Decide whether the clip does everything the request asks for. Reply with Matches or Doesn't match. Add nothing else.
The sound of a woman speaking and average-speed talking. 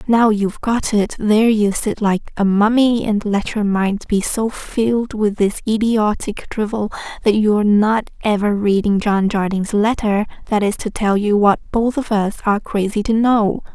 Matches